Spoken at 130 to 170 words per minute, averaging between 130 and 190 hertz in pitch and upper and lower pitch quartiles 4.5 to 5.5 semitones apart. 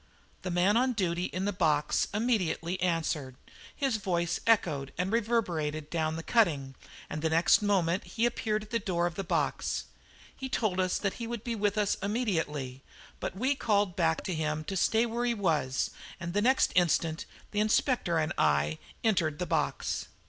No: average, 180 wpm; medium, 185 Hz; average, 5.0 semitones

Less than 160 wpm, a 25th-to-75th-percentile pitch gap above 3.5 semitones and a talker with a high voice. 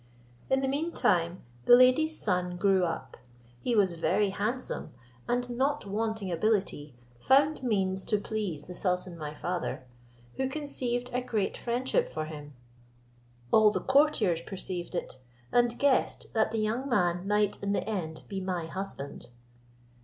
Yes: average, 150 wpm; wide, 5.5 semitones; high, 205 Hz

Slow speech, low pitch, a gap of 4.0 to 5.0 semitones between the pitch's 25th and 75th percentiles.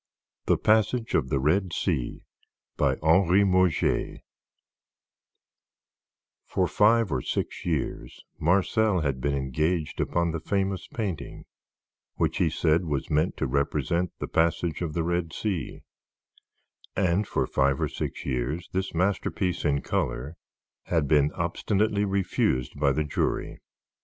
Yes: slow, 130 wpm; very low, 85 Hz; average, 4.5 semitones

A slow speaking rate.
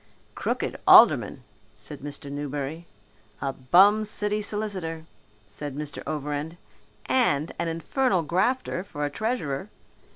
Yes: slow, 105 wpm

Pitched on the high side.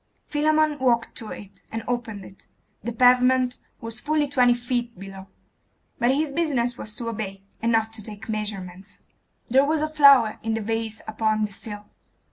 Yes: high, 230 Hz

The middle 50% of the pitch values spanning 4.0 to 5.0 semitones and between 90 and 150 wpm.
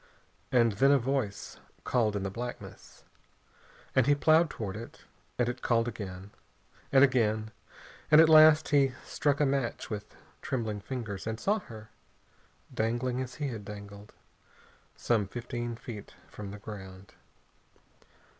Yes: average, 4.3 semitones; average, 140 wpm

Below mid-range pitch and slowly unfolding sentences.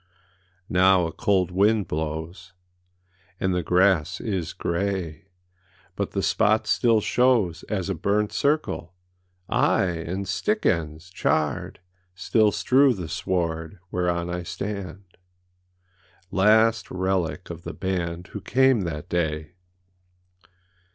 Yes: very low, 95 Hz; slow, 110 wpm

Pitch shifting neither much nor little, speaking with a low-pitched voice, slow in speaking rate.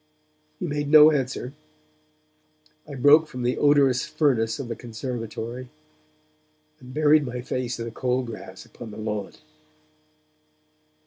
Yes: average, 3.7 semitones; low, 125 Hz; slow, 130 wpm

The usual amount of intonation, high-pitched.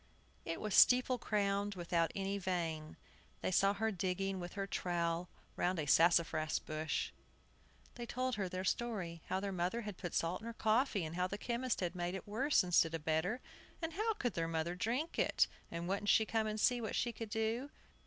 Yes: average, 4.4 semitones; high, 195 Hz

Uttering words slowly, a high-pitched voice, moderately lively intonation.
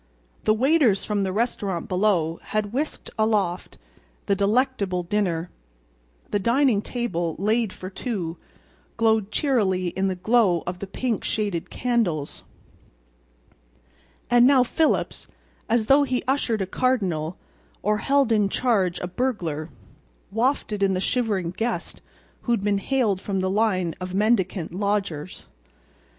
Yes: slow, 130 wpm; high, 205 Hz; average, 4.5 semitones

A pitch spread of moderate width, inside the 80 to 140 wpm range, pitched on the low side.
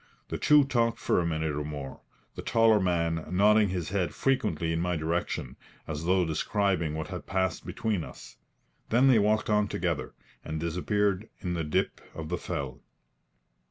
No: average, 4.5 semitones; average, 170 wpm; very low, 90 Hz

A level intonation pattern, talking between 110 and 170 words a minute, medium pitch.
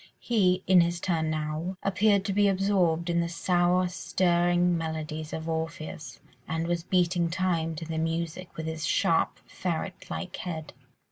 Yes: narrow, 2.2 semitones; average, 155 wpm; medium, 170 Hz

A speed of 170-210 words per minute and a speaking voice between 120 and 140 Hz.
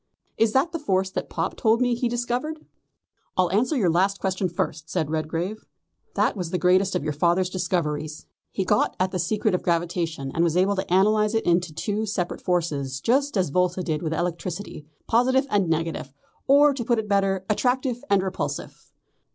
No: average, 185 wpm; medium, 185 Hz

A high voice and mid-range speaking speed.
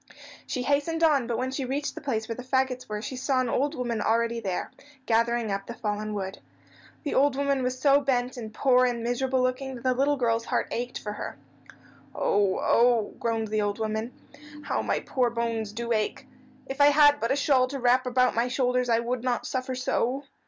No: very high, 250 Hz; fast, 210 wpm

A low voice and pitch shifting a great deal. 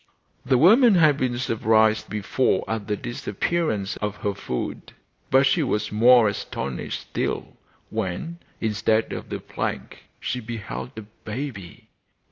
No: low, 110 Hz; average, 3.9 semitones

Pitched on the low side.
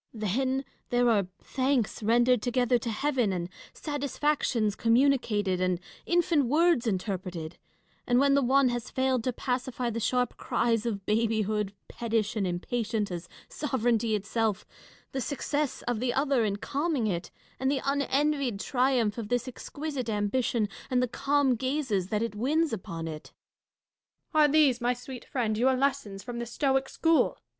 No: high, 245 Hz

